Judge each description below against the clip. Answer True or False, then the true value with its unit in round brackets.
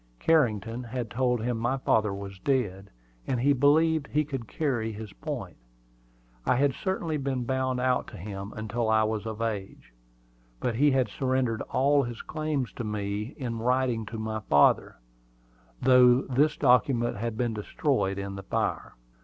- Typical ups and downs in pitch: True (3.5 semitones)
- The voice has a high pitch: False (120 Hz)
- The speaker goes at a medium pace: True (160 wpm)